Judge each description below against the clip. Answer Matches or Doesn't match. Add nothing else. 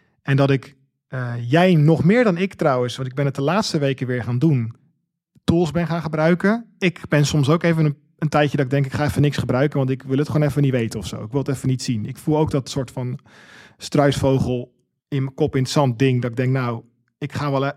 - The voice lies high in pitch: Doesn't match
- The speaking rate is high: Matches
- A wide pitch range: Doesn't match